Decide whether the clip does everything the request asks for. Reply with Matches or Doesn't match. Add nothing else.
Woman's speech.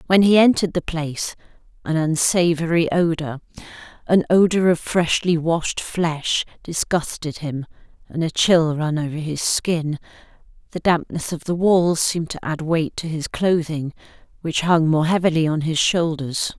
Matches